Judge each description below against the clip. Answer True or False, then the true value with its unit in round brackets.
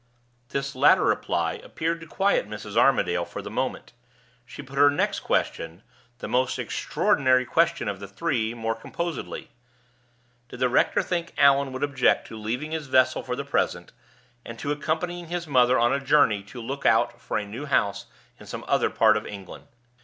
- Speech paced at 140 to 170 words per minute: False (180 wpm)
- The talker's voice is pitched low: True (130 Hz)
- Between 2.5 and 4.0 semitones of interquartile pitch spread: False (4.6 semitones)